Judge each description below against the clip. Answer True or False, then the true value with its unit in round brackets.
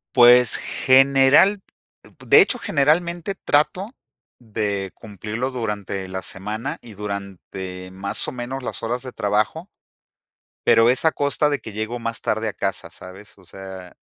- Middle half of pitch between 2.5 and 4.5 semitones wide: False (5.2 semitones)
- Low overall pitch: True (115 Hz)